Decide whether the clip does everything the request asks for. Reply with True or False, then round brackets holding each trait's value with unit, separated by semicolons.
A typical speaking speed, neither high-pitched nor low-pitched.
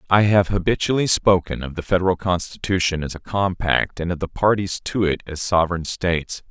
False (185 wpm; 90 Hz)